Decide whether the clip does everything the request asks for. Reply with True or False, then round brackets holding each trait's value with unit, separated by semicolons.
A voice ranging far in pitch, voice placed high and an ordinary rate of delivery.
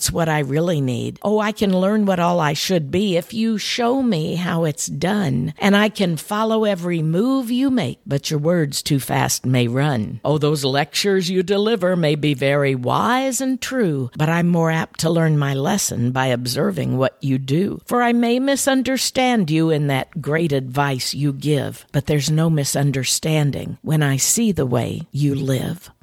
False (6.2 semitones; 160 Hz; 185 wpm)